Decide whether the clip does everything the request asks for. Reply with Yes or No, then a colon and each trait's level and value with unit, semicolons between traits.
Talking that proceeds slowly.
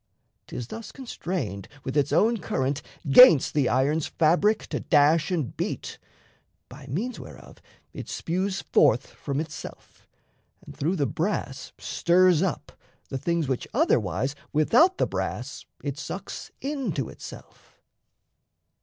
Yes: slow, 125 wpm